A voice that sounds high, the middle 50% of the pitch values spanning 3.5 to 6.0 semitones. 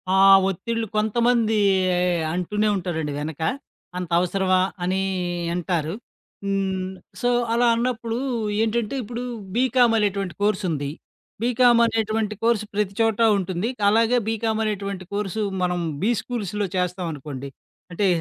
Yes: high, 205 Hz; average, 3.8 semitones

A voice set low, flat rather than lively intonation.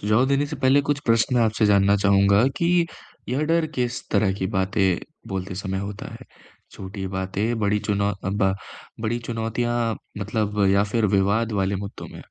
No: low, 105 Hz; average, 3.3 semitones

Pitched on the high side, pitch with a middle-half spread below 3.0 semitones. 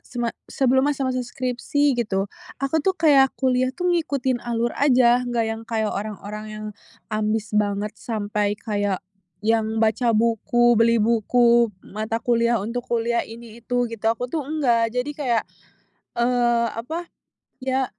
Yes: high, 235 Hz; narrow, 2.5 semitones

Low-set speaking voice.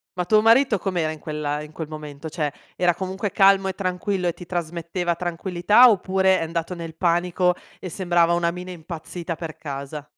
No: medium, 175 Hz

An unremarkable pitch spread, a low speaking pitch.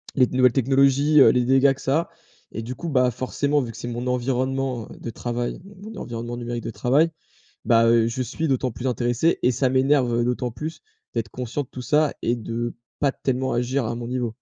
No: narrow, 2.2 semitones; low, 125 Hz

